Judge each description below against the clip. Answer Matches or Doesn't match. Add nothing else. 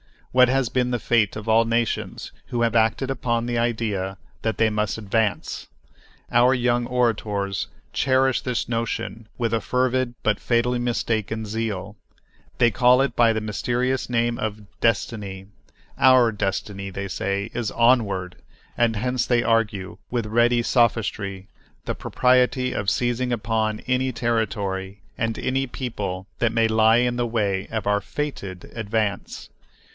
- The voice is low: Matches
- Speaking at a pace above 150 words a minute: Doesn't match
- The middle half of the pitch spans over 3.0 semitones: Doesn't match